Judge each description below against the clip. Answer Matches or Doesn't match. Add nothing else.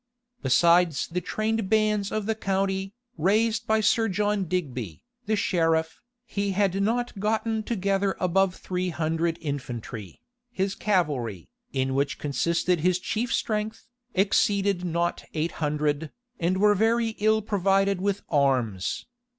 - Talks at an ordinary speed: Doesn't match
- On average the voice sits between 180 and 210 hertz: Matches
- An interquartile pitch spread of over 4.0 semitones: Matches